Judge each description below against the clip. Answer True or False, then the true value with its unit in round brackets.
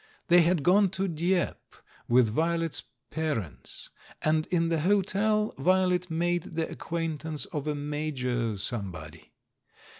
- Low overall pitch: False (160 Hz)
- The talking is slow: True (125 wpm)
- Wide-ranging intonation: False (3.7 semitones)